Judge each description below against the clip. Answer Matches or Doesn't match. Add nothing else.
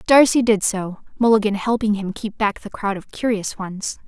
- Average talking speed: Matches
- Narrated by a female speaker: Matches